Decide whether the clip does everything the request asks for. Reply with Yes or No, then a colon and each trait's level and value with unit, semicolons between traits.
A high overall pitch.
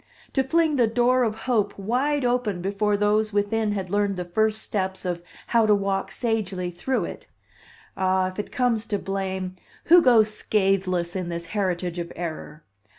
Yes: high, 205 Hz